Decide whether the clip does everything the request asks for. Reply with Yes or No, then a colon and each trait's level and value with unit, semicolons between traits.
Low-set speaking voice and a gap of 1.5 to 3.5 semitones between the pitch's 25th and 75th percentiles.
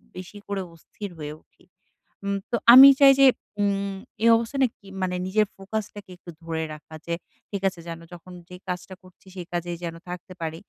No: medium, 185 Hz; average, 2.8 semitones